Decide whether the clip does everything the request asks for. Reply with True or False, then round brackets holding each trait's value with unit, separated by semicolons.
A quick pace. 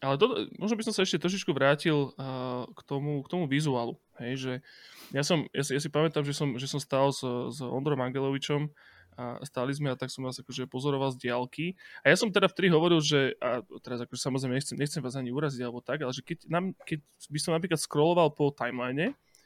True (215 wpm)